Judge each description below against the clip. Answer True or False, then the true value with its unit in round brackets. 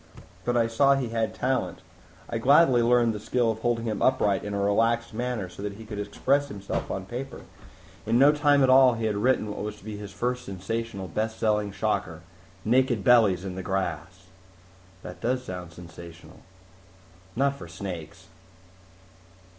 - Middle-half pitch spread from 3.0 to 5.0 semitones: True (4.0 semitones)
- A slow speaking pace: False (175 wpm)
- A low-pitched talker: True (110 Hz)